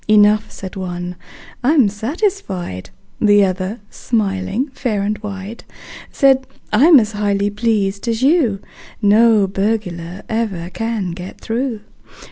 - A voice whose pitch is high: Yes, high, 210 Hz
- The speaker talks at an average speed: No, slow, 115 wpm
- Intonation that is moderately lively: Yes, average, 3.1 semitones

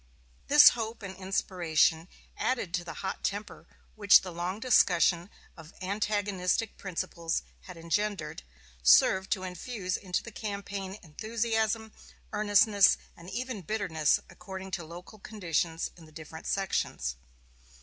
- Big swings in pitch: No, average, 3.7 semitones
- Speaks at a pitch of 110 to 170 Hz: No, high, 190 Hz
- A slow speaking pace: Yes, slow, 125 wpm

